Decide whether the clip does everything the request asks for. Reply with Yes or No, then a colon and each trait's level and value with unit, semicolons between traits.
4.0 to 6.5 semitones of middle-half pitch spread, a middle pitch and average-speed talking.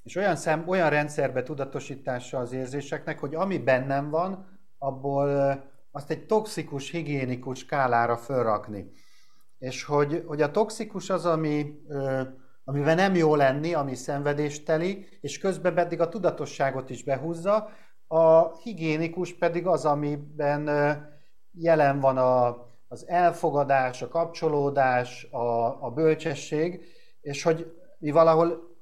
No: average, 3.5 semitones; medium, 150 Hz; average, 120 wpm